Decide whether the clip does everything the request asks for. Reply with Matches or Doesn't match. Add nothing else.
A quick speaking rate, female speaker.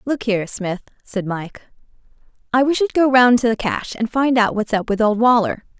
Matches